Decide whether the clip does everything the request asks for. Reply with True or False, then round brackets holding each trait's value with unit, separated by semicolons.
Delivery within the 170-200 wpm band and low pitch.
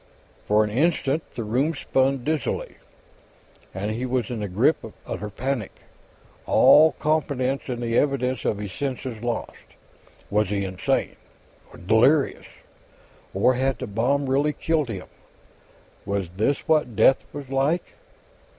False (140 wpm; 125 Hz)